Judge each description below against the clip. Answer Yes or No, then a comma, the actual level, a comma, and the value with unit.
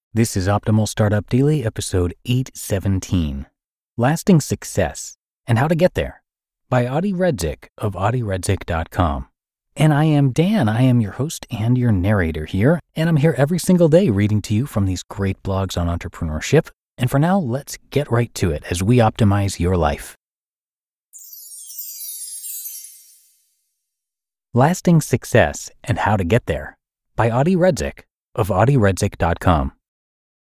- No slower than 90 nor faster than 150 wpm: Yes, average, 140 wpm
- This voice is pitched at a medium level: No, low, 110 Hz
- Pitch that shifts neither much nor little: No, wide, 6.4 semitones